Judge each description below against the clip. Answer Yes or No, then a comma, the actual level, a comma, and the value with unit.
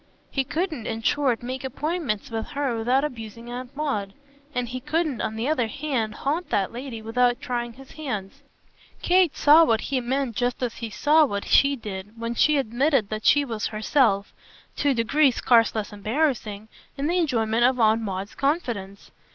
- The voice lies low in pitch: No, high, 245 Hz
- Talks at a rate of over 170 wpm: Yes, average, 180 wpm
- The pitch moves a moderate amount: Yes, average, 4.2 semitones